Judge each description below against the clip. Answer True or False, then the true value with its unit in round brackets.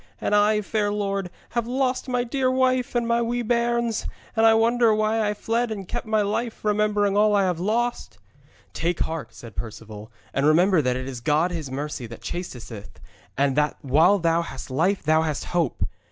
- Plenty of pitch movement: True (7.0 semitones)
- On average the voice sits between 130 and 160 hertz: False (205 Hz)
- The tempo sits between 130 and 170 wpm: False (190 wpm)